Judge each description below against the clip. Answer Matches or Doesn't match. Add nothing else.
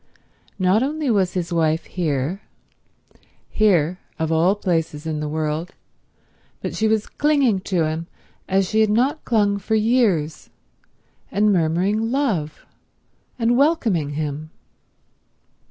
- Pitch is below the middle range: Doesn't match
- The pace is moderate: Doesn't match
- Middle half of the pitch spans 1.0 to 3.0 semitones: Doesn't match